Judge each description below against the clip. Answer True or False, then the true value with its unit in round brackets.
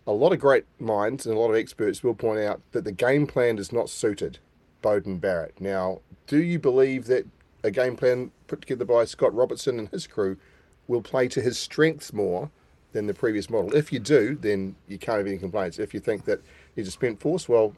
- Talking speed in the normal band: False (225 wpm)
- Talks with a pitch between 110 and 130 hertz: True (115 Hz)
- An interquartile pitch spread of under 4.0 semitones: False (4.5 semitones)